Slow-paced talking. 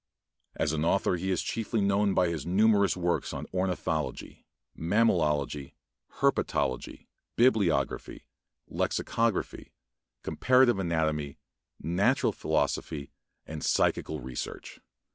Yes: slow, 95 wpm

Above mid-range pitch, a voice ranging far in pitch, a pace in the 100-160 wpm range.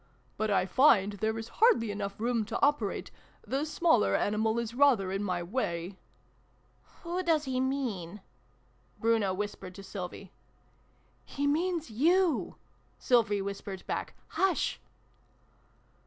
Yes: high, 220 Hz; wide, 6.1 semitones; average, 140 wpm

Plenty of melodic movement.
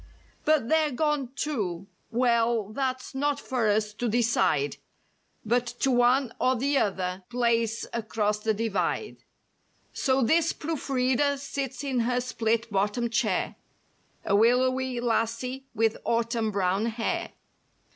No: average, 3.1 semitones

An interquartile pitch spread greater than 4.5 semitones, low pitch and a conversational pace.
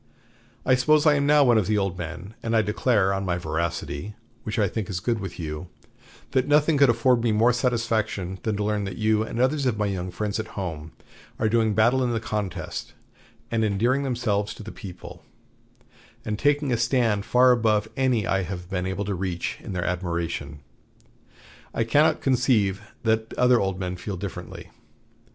No: average, 4.2 semitones; low, 105 Hz; average, 190 wpm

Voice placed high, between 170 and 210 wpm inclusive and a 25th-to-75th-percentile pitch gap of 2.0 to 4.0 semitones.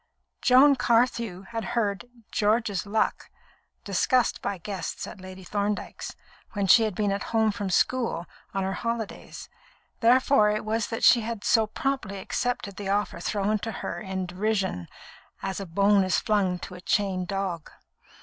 No: high, 205 Hz; average, 160 wpm; average, 2.9 semitones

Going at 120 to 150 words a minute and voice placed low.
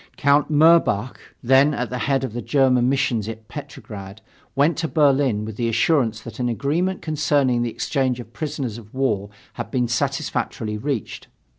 No: average, 165 wpm; low, 130 Hz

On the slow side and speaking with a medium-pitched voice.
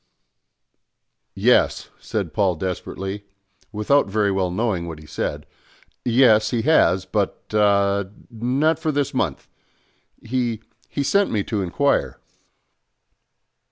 No: slow, 115 wpm; low, 105 Hz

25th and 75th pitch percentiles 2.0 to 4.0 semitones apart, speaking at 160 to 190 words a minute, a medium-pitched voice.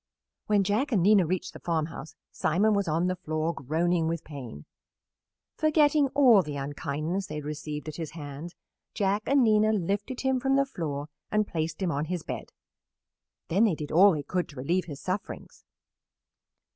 No: average, 5.3 semitones; average, 175 wpm; medium, 175 Hz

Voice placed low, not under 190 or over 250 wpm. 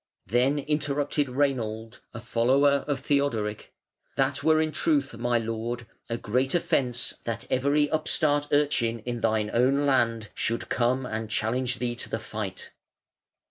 No: low, 125 Hz; average, 140 wpm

